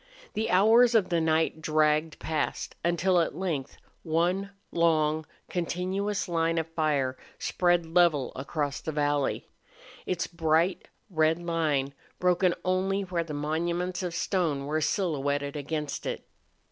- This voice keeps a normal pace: No, slow, 130 wpm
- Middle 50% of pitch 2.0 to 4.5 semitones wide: Yes, average, 2.8 semitones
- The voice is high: No, medium, 165 Hz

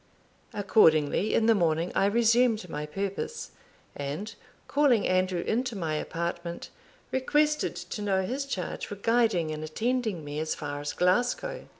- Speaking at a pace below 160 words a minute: Yes, average, 140 wpm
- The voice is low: No, high, 195 Hz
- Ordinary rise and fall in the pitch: No, wide, 6.4 semitones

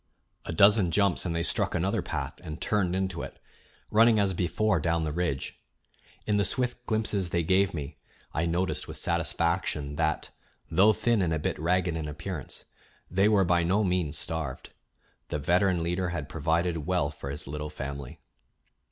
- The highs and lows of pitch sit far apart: No, average, 3.4 semitones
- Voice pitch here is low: Yes, very low, 85 Hz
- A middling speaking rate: Yes, average, 170 wpm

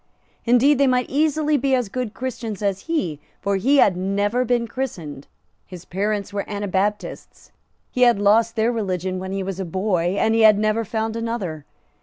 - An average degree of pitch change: Yes, average, 4.1 semitones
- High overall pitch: Yes, high, 215 Hz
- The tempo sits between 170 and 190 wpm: Yes, average, 180 wpm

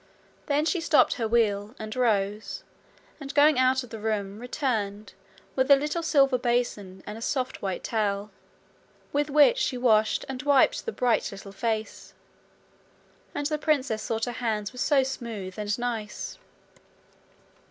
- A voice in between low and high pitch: No, high, 240 Hz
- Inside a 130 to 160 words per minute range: Yes, average, 155 wpm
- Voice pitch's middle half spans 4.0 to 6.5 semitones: Yes, average, 4.5 semitones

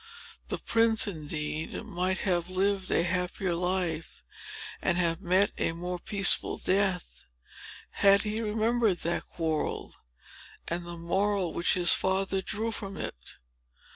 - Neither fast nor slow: No, slow, 130 wpm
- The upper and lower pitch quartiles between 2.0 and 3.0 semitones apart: Yes, average, 2.7 semitones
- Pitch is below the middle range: No, medium, 185 Hz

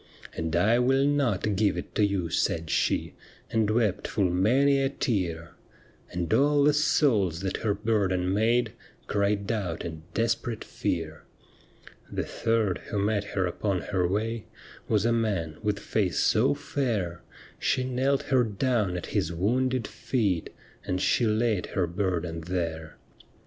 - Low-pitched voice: Yes, low, 105 Hz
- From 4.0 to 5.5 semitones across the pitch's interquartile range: Yes, average, 4.7 semitones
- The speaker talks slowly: No, average, 150 wpm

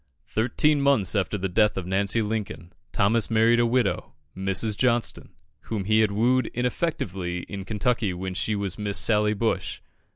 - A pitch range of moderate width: Yes, average, 3.2 semitones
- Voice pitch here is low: Yes, low, 105 Hz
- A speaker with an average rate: Yes, average, 160 wpm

